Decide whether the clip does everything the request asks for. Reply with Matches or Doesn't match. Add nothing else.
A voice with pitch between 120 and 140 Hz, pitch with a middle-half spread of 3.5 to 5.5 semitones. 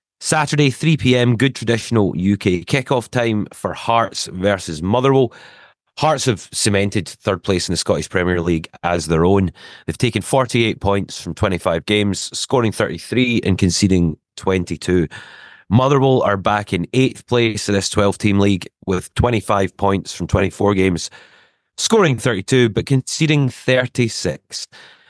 Doesn't match